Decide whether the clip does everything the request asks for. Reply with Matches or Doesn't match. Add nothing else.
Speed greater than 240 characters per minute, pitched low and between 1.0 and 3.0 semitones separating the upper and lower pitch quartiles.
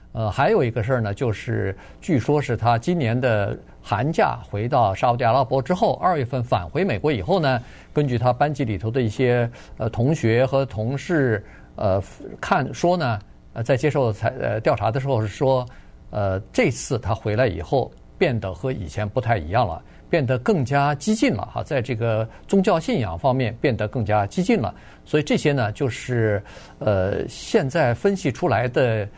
Doesn't match